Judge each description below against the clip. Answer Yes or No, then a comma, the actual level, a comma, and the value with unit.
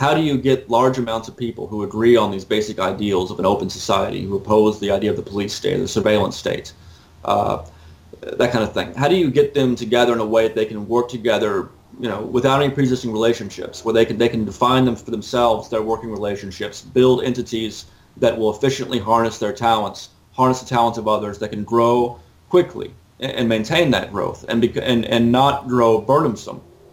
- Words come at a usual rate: No, fast, 210 wpm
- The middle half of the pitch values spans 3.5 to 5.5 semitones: No, average, 2.8 semitones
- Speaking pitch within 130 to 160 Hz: No, low, 115 Hz